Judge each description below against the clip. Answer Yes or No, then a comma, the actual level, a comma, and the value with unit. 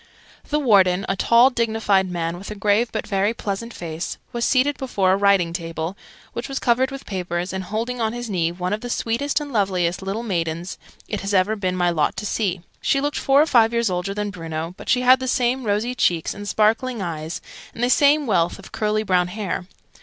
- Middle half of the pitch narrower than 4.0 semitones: No, average, 4.7 semitones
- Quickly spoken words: Yes, fast, 215 wpm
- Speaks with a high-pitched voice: Yes, high, 205 Hz